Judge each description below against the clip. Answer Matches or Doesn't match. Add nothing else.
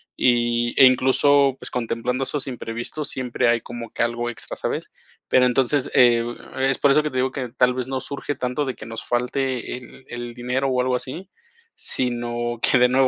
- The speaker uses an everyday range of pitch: Doesn't match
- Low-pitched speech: Matches